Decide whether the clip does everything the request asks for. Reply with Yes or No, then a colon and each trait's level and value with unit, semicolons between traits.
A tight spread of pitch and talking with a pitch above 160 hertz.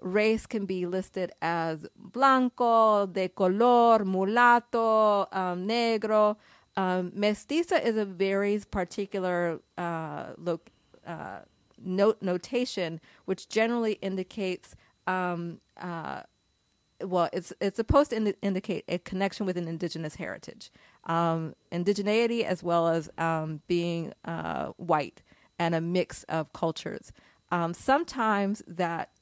No: average, 3.9 semitones; high, 190 Hz